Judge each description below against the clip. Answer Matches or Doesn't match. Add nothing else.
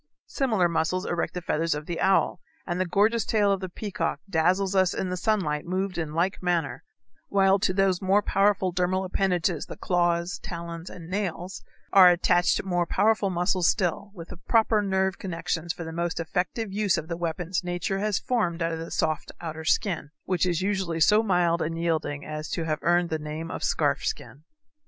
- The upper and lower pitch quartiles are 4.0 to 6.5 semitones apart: Doesn't match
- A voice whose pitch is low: Doesn't match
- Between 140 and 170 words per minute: Doesn't match